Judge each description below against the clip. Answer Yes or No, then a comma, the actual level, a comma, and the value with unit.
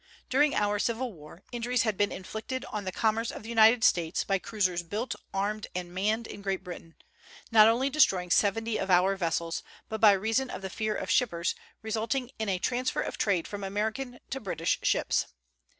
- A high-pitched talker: Yes, high, 215 Hz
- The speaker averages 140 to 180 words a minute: No, average, 190 wpm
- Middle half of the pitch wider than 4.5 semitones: No, average, 3.4 semitones